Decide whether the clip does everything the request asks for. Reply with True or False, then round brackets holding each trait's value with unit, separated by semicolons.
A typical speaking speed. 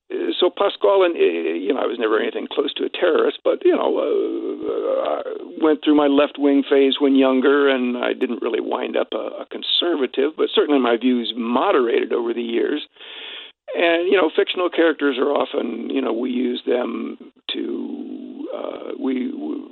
True (185 wpm)